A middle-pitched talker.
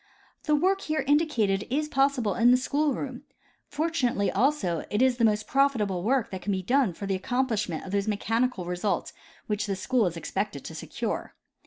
No: high, 230 Hz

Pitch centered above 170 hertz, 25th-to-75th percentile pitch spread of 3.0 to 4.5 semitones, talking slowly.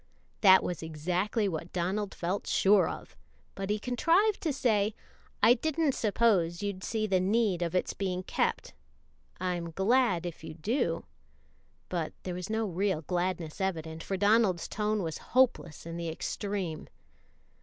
No: high, 190 Hz; average, 3.9 semitones; average, 150 wpm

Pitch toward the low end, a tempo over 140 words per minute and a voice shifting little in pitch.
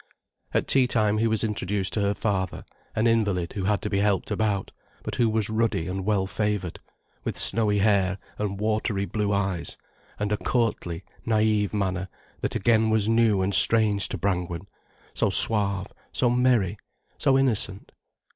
Yes: low, 105 Hz; average, 165 wpm; narrow, 2.3 semitones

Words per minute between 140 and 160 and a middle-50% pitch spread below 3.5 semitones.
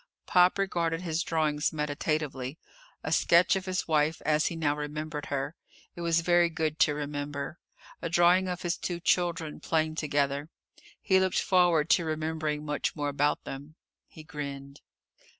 Yes: average, 155 wpm; narrow, 2.6 semitones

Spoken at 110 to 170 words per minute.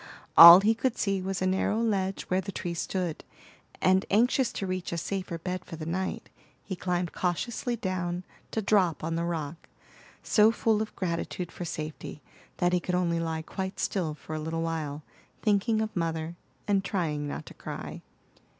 No: average, 180 wpm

